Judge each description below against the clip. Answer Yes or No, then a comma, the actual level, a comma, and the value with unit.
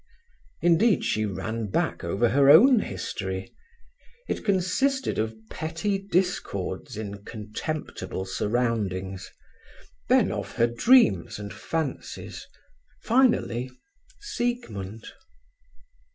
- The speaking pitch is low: Yes, low, 120 Hz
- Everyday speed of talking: No, slow, 85 wpm